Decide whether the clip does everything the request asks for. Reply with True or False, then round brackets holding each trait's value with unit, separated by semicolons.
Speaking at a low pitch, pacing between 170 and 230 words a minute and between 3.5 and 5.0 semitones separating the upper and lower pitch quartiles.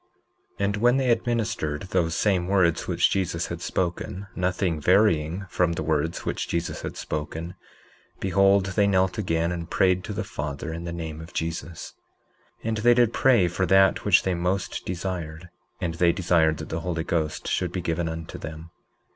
False (90 Hz; 180 wpm; 2.9 semitones)